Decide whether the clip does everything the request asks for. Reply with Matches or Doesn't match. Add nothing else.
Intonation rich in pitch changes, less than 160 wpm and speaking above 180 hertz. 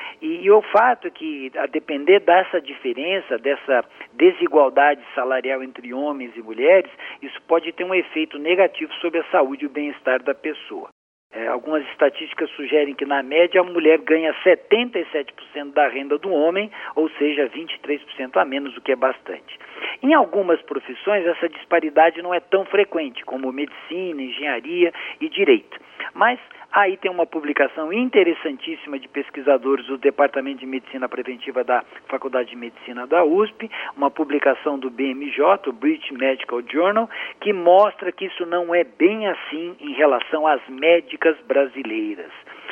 Doesn't match